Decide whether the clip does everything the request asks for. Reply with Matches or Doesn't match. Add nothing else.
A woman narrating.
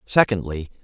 Doesn't match